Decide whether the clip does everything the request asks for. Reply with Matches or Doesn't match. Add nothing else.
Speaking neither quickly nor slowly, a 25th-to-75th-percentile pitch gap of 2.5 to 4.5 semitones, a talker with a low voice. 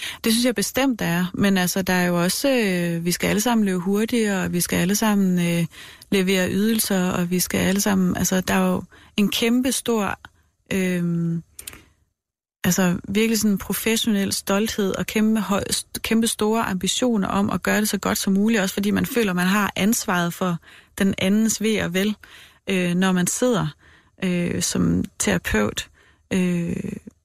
Doesn't match